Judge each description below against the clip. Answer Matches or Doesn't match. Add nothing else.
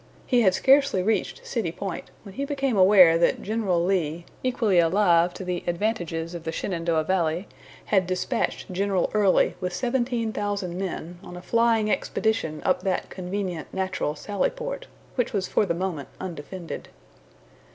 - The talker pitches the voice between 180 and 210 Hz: Matches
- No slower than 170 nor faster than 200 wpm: Doesn't match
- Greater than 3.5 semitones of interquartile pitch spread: Matches